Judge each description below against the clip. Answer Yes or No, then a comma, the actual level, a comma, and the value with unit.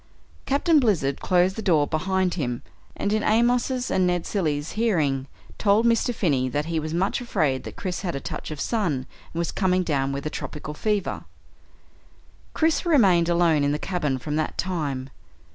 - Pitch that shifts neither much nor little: No, wide, 5.9 semitones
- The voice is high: No, medium, 175 Hz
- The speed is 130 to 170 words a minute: No, average, 180 wpm